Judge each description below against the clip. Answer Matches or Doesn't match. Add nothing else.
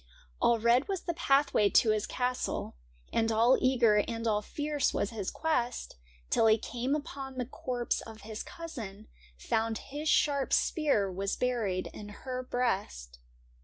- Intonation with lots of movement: Doesn't match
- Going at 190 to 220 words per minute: Doesn't match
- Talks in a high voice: Matches